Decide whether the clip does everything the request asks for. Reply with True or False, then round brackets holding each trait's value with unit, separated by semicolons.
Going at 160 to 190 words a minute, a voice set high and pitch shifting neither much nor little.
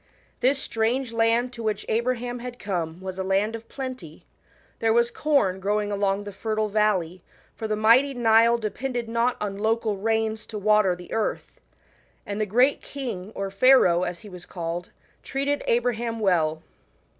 True (170 wpm; 220 Hz; 3.4 semitones)